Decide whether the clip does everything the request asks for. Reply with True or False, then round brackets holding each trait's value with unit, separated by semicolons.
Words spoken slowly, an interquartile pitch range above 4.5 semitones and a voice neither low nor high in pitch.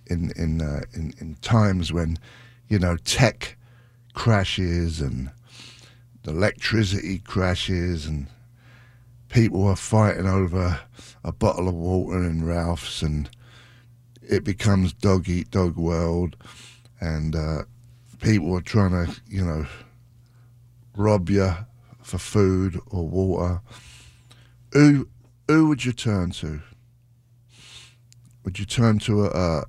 False (120 wpm; 5.4 semitones; 100 Hz)